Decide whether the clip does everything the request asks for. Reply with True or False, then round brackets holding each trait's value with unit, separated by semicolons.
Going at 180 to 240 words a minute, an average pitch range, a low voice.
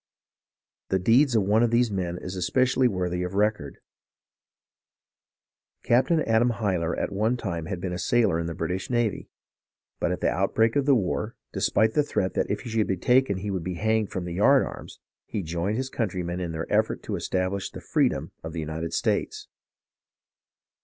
True (185 wpm; 4.5 semitones; 100 Hz)